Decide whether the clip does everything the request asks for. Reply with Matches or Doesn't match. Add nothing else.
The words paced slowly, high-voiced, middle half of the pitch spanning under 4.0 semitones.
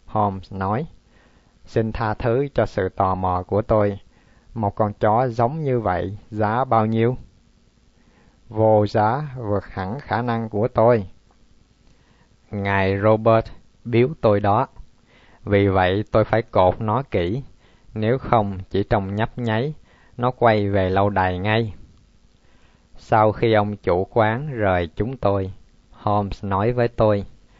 Doesn't match